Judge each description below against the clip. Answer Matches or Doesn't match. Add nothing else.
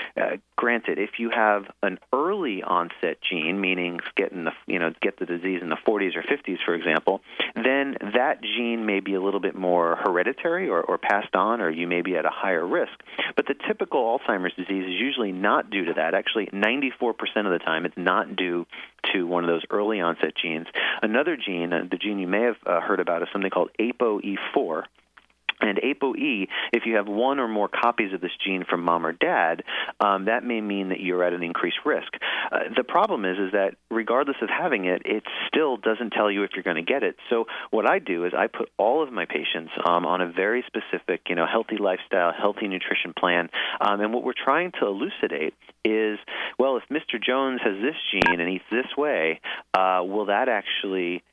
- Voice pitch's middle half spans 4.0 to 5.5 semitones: Doesn't match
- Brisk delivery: Matches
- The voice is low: Matches